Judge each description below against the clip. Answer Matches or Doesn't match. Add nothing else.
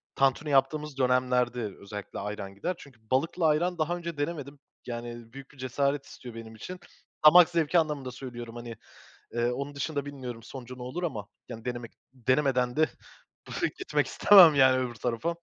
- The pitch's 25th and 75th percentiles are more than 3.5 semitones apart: Matches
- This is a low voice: Matches